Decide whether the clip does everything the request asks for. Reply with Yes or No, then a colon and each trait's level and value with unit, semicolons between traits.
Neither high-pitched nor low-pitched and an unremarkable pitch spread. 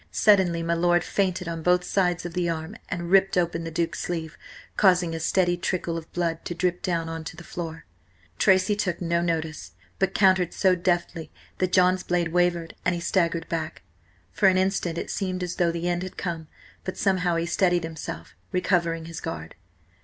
No: medium, 175 Hz; narrow, 1.7 semitones